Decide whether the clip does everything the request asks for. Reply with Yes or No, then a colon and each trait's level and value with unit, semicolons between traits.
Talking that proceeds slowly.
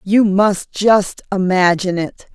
Yes: slow, 130 wpm